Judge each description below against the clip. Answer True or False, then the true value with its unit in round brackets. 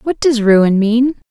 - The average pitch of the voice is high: True (235 Hz)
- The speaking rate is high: False (185 wpm)